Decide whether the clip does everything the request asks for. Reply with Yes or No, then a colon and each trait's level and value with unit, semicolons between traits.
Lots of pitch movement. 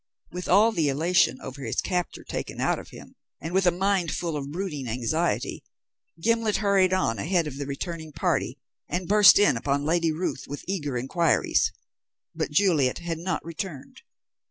No: average, 4.5 semitones